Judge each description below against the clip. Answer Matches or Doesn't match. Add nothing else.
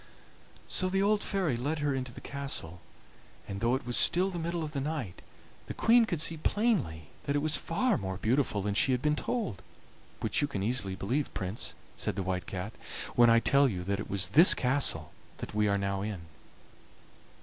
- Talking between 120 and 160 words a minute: Doesn't match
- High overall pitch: Doesn't match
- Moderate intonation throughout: Doesn't match